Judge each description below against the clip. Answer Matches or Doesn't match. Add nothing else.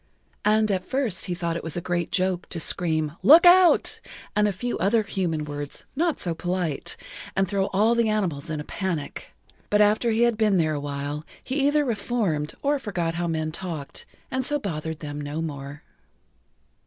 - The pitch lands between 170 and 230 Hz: Matches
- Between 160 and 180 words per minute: Doesn't match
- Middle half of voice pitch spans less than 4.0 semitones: Doesn't match